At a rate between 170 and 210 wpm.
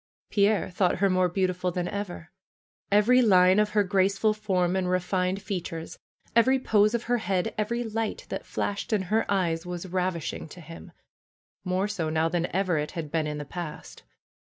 Yes: average, 180 wpm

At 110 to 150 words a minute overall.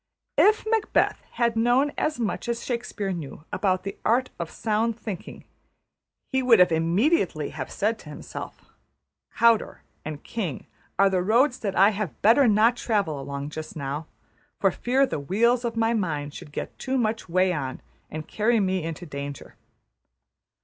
No: average, 160 wpm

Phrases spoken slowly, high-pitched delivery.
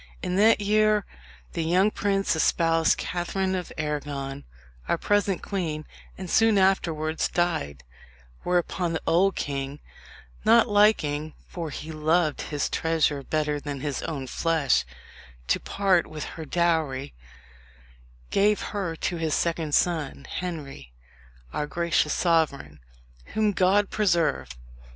No: slow, 125 wpm; medium, 165 Hz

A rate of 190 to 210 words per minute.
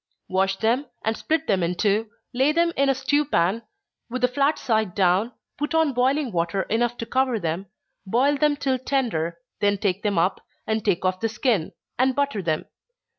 Yes: average, 195 wpm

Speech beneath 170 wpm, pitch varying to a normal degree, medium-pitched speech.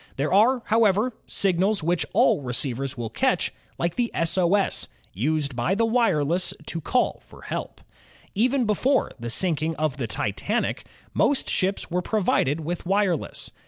No: average, 155 wpm; wide, 6.3 semitones; medium, 175 Hz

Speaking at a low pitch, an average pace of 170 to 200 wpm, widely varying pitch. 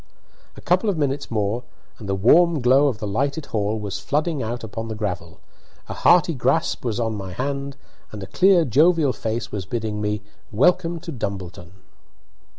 Yes: low, 120 Hz; average, 175 wpm; wide, 6.1 semitones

